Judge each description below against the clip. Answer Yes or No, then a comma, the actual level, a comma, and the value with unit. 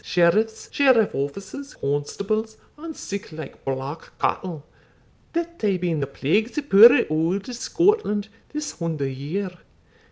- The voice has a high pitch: Yes, high, 195 Hz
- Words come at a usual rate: No, slow, 125 wpm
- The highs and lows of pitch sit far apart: Yes, wide, 7.3 semitones